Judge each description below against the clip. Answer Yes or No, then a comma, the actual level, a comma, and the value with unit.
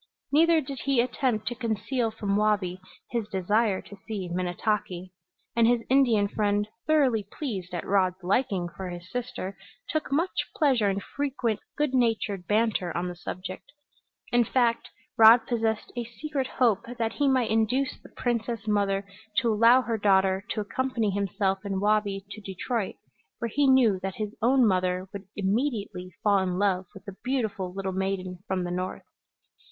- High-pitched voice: Yes, high, 210 Hz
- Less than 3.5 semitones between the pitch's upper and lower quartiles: No, average, 4.0 semitones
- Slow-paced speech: No, average, 165 wpm